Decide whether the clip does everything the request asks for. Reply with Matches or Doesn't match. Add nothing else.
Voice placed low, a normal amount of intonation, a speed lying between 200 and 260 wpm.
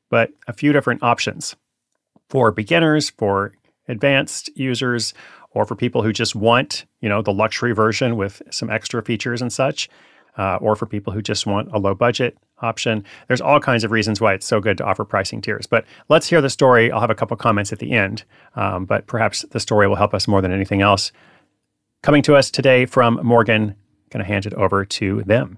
Matches